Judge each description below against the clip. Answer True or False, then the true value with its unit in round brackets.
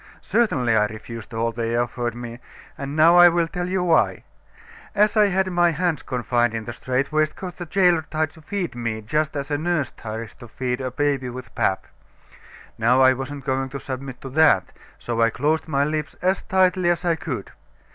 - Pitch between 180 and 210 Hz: False (140 Hz)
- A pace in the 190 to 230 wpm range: True (195 wpm)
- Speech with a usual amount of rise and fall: False (6.0 semitones)